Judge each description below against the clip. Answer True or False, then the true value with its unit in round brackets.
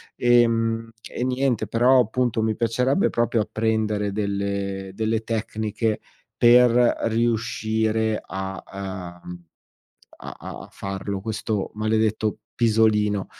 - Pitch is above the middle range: False (110 Hz)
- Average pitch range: False (1.9 semitones)